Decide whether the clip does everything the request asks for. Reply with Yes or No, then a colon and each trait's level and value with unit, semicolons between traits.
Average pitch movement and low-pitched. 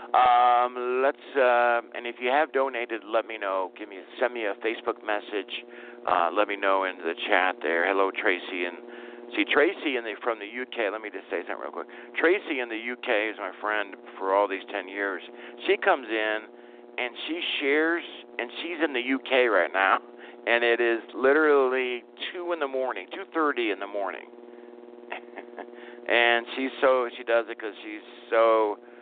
No: narrow, 2.2 semitones; low, 120 Hz